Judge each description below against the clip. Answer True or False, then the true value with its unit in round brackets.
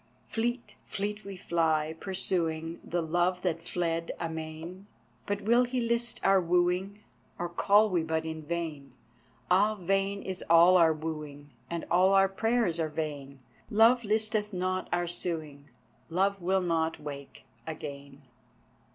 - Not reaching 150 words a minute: True (140 wpm)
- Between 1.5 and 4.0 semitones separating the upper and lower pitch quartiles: True (3.5 semitones)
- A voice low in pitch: False (175 Hz)